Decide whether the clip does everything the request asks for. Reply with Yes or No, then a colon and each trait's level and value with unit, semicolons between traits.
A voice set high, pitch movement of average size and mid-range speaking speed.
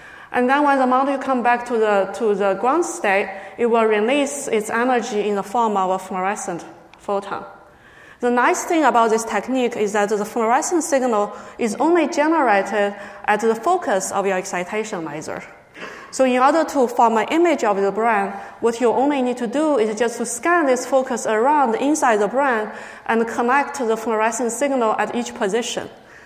Yes: high, 235 Hz; average, 4.1 semitones; average, 185 wpm